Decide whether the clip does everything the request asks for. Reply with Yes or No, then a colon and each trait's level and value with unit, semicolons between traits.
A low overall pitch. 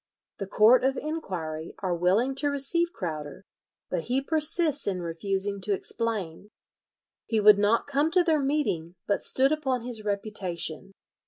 No: high, 215 Hz